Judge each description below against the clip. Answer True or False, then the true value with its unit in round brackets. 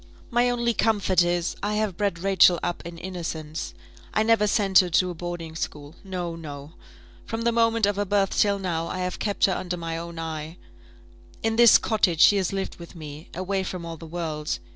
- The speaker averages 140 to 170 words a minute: False (205 wpm)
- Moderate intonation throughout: True (3.6 semitones)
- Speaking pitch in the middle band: True (180 Hz)